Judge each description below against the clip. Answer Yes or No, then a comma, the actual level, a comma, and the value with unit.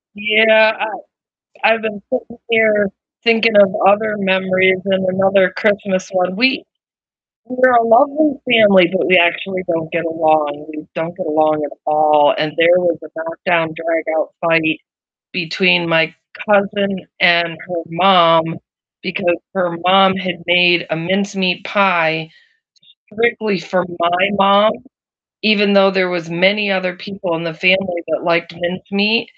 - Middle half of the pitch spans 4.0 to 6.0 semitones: No, average, 3.3 semitones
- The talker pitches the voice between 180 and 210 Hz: Yes, medium, 185 Hz